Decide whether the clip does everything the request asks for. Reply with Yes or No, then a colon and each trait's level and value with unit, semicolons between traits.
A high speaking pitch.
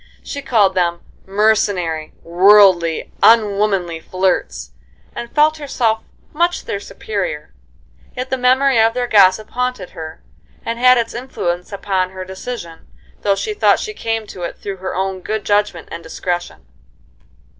Yes: high, 200 Hz